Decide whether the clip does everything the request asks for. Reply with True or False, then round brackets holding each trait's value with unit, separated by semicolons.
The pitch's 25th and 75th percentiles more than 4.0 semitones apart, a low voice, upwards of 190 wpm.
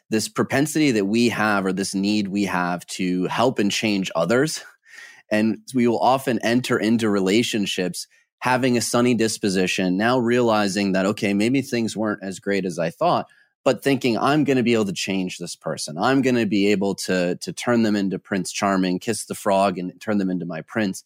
False (3.6 semitones; 105 Hz; 200 wpm)